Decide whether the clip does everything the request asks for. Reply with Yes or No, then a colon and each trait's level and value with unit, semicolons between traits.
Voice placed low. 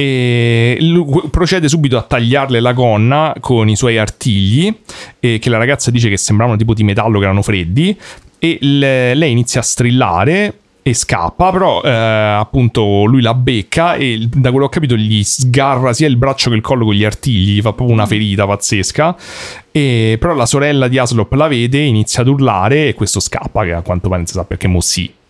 Yes: low, 120 Hz